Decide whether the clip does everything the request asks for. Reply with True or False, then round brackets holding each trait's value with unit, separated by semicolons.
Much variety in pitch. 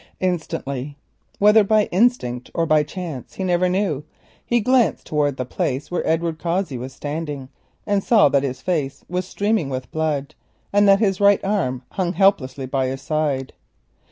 True (6.0 semitones)